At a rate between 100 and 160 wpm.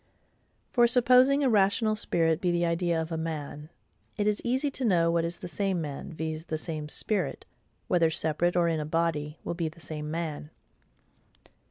No: average, 175 wpm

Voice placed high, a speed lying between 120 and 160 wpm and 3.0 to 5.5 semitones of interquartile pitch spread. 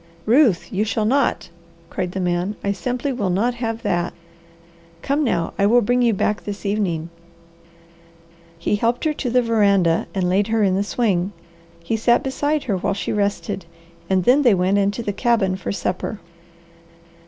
No: high, 205 Hz; average, 175 wpm; average, 4.0 semitones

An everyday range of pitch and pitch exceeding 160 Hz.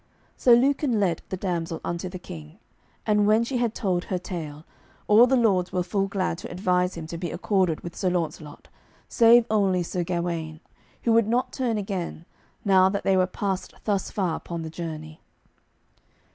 Yes: average, 3.5 semitones; medium, 185 Hz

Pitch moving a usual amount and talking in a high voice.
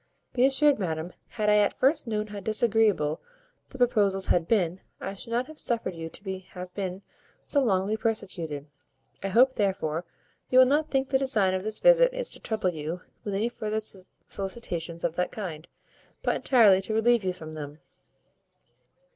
Yes: average, 4.8 semitones; high, 205 Hz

